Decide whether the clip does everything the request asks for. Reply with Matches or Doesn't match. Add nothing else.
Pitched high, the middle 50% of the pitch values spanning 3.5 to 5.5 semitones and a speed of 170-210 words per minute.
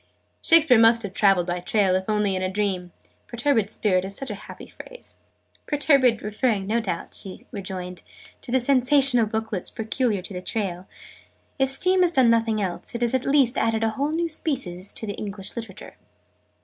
Matches